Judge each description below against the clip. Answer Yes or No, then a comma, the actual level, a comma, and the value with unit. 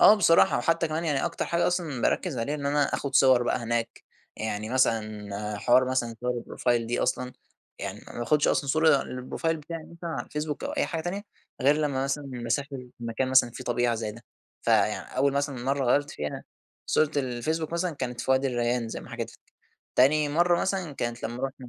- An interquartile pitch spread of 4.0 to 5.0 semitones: Yes, average, 4.3 semitones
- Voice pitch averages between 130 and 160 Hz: Yes, low, 135 Hz